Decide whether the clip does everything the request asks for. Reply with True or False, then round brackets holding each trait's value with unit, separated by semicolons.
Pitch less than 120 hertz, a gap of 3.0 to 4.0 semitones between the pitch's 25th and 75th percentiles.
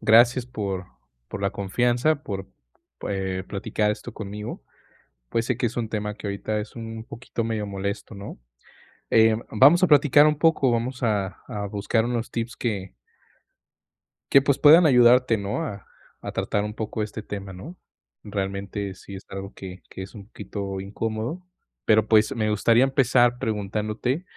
True (110 Hz; 3.4 semitones)